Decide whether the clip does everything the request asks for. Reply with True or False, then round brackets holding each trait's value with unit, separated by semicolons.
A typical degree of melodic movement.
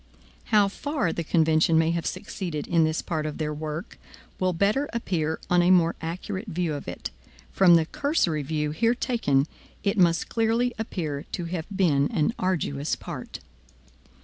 True (4.1 semitones)